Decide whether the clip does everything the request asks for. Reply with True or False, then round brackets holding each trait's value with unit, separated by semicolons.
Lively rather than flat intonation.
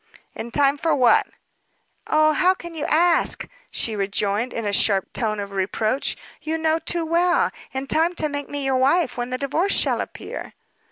True (5.9 semitones)